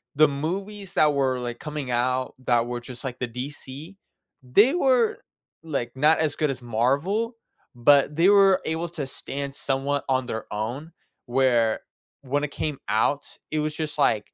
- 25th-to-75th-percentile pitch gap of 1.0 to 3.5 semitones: No, average, 4.0 semitones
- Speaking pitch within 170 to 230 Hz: No, medium, 140 Hz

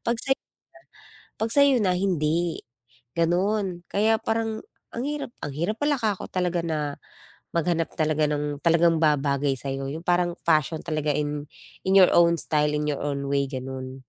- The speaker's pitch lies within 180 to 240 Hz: No, medium, 165 Hz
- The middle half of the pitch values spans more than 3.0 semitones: Yes, average, 4.5 semitones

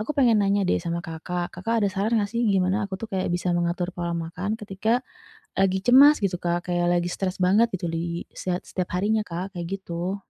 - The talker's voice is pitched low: No, high, 190 Hz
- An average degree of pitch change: Yes, average, 3.0 semitones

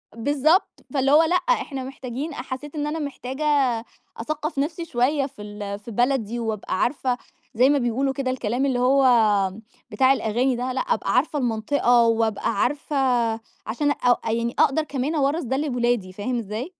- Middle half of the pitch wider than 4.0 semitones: No, average, 3.4 semitones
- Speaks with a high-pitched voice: Yes, very high, 260 Hz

